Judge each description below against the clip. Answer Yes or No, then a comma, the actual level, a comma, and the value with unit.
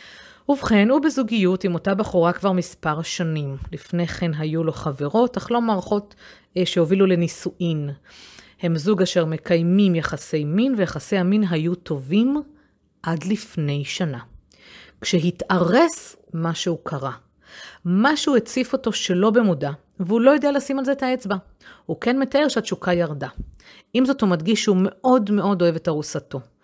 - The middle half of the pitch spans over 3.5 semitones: Yes, average, 5.1 semitones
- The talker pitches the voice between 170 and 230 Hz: Yes, medium, 185 Hz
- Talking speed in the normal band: Yes, average, 140 wpm